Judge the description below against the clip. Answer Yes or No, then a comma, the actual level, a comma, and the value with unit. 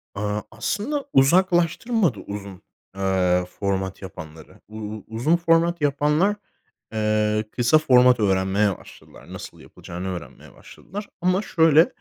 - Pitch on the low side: Yes, low, 110 Hz